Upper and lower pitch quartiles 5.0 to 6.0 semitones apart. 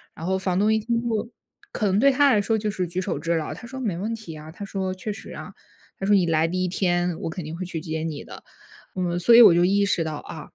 No: average, 4.0 semitones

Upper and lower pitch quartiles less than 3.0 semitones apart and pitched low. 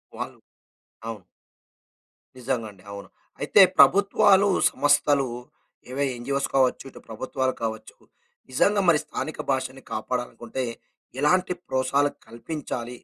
No: average, 3.3 semitones; low, 130 Hz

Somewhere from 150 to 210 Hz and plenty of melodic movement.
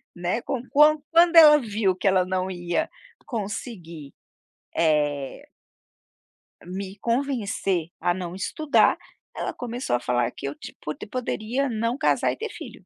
Yes: high, 200 Hz; wide, 6.4 semitones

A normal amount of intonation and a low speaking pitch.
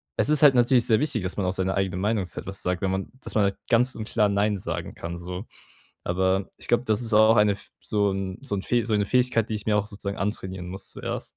Yes: average, 3.0 semitones; low, 105 Hz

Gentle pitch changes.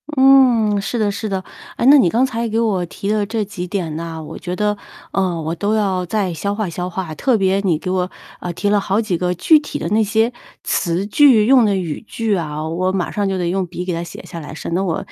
No: average, 3.6 semitones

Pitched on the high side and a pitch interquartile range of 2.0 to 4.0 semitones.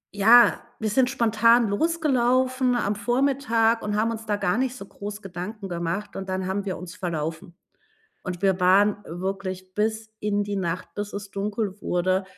Yes: high, 205 Hz; average, 3.4 semitones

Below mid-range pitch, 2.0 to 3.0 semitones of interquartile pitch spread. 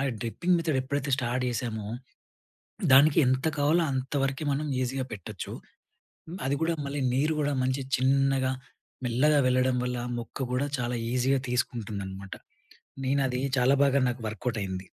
Yes: low, 130 Hz; narrow, 2.5 semitones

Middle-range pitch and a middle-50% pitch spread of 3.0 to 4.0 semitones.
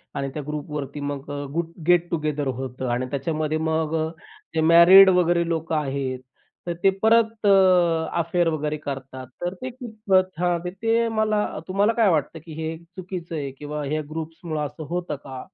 Yes: medium, 160 Hz; average, 3.6 semitones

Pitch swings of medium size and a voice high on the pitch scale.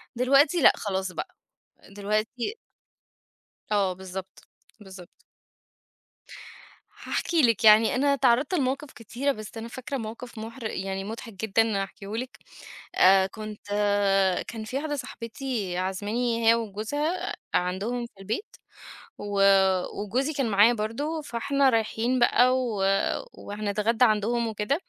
Yes: average, 3.7 semitones; high, 225 Hz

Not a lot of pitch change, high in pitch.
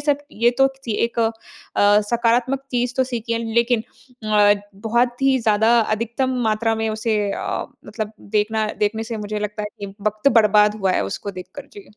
Yes: narrow, 2.3 semitones; high, 225 Hz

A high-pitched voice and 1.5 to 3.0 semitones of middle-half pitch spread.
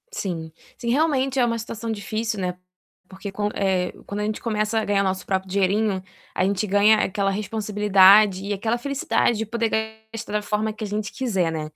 Yes: high, 210 Hz; narrow, 2.5 semitones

